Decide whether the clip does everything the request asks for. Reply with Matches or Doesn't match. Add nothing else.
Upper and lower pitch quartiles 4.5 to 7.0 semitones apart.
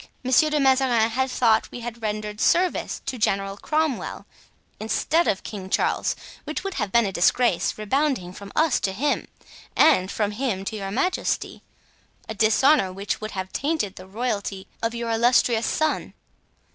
Matches